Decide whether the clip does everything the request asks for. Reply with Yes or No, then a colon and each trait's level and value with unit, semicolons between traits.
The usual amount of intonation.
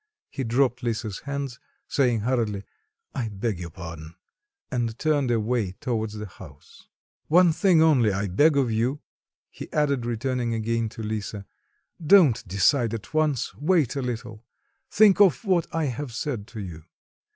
Yes: average, 4.8 semitones